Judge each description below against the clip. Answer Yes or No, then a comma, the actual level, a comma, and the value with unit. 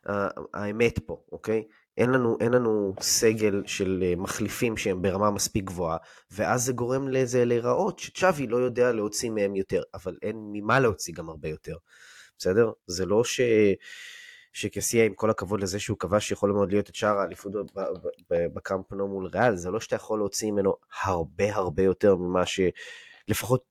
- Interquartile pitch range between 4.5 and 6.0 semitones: No, average, 3.3 semitones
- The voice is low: Yes, low, 105 Hz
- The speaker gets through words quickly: Yes, fast, 160 wpm